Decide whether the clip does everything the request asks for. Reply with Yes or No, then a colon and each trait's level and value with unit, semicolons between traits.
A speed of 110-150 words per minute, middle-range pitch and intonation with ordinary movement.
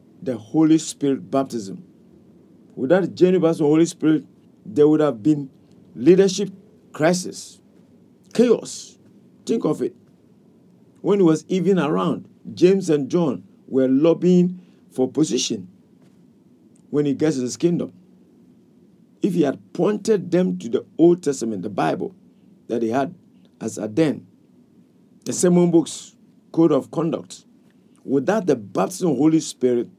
Yes: slow, 135 wpm; medium, 160 Hz; average, 4.3 semitones